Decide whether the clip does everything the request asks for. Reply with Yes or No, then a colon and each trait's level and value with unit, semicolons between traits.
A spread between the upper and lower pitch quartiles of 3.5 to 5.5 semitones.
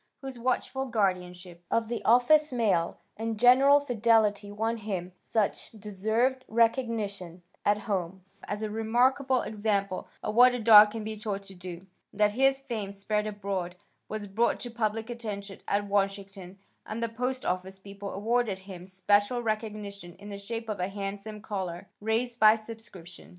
No: average, 2.7 semitones